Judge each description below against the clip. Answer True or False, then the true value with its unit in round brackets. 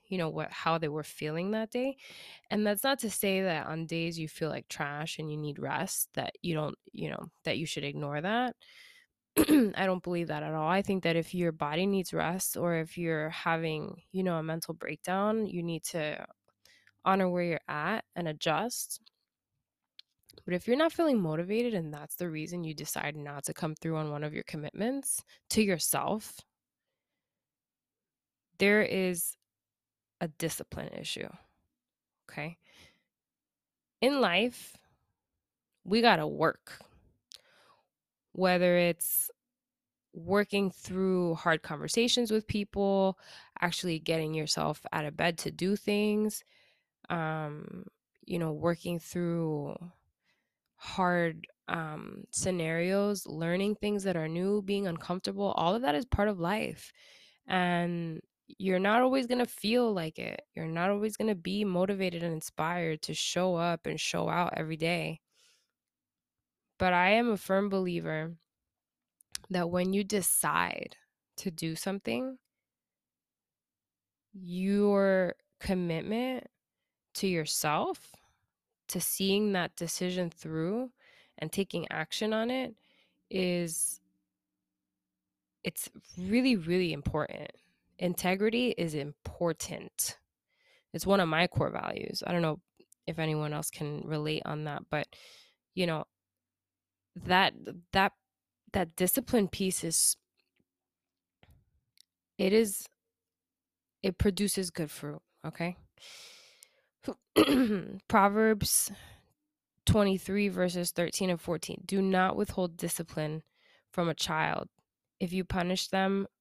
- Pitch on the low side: False (180 Hz)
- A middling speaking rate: False (130 wpm)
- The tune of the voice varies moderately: True (4.0 semitones)